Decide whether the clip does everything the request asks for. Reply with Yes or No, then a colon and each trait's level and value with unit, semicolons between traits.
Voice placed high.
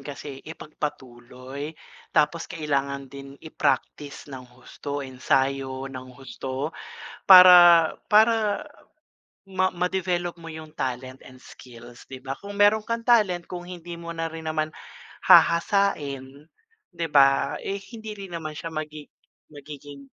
No: medium, 155 Hz